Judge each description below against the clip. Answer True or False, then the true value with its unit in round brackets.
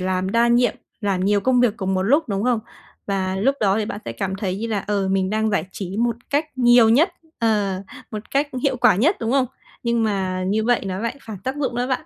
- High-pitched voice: True (220 Hz)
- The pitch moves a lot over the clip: False (3.9 semitones)